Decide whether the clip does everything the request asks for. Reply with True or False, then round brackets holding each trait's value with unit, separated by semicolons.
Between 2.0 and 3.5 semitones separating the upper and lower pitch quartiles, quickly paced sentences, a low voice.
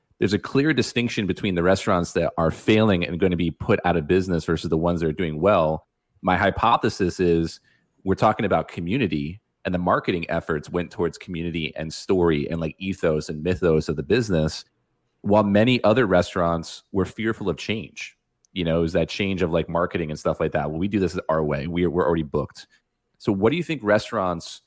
True (3.2 semitones; 210 wpm; 85 Hz)